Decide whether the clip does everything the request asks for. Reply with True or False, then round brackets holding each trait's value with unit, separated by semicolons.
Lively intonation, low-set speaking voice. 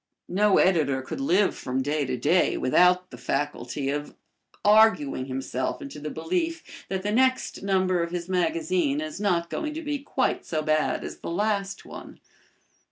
False (7.0 semitones; 180 Hz)